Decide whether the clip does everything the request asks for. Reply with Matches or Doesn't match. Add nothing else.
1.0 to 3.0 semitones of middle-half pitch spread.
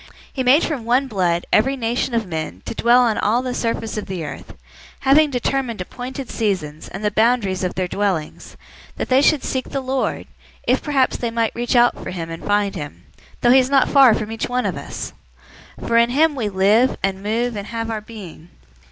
Doesn't match